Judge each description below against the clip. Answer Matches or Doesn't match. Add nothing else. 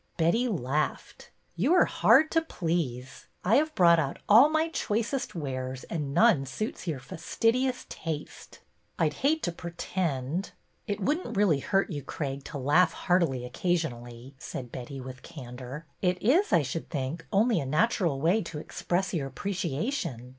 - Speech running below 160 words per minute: Doesn't match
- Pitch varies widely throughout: Matches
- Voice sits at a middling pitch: Matches